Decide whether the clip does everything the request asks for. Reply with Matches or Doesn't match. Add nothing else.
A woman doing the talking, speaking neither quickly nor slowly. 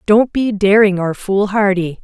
Matches